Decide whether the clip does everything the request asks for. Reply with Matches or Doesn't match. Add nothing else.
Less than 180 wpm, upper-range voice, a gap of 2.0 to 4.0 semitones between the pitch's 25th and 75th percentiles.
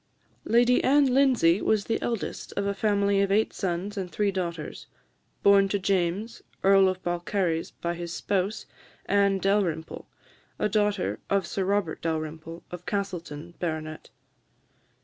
Matches